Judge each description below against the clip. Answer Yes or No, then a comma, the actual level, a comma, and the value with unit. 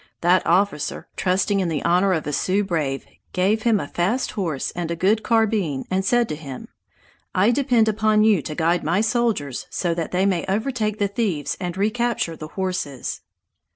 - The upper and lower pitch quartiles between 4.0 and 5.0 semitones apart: Yes, average, 4.5 semitones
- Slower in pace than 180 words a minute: No, average, 185 wpm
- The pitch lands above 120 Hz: Yes, high, 190 Hz